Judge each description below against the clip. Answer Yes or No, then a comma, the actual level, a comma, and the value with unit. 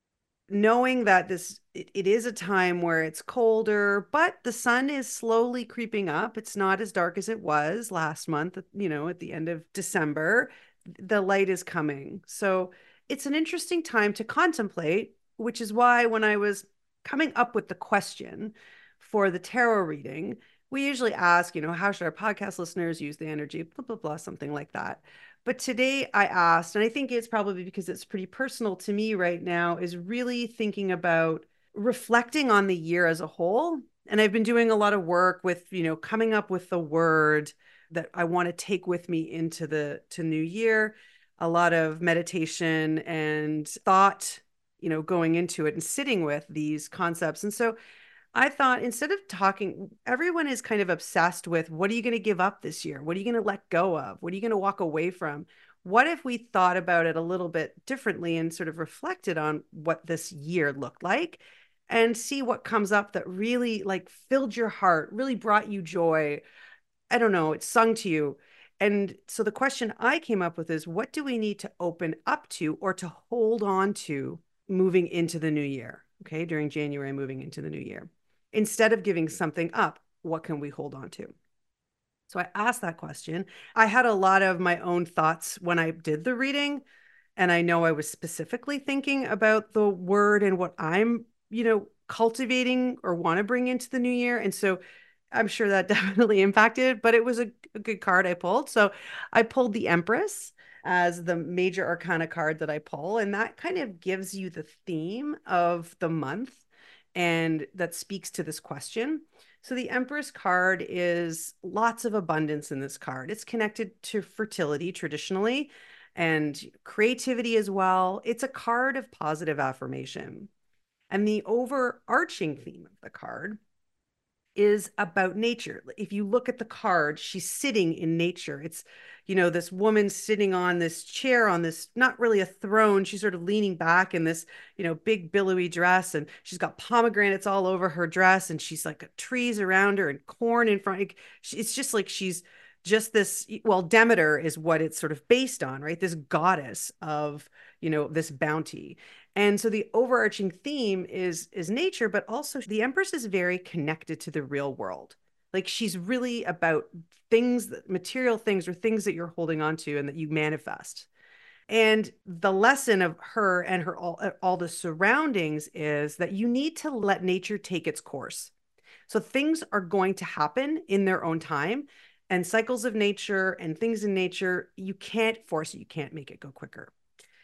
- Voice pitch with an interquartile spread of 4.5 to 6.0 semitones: Yes, average, 5.1 semitones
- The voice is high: Yes, high, 195 Hz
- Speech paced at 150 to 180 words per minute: No, average, 190 wpm